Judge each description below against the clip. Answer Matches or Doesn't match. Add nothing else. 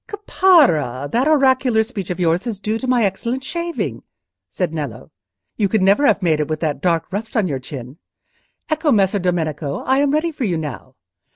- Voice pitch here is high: Matches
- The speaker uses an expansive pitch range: Matches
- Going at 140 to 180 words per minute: Doesn't match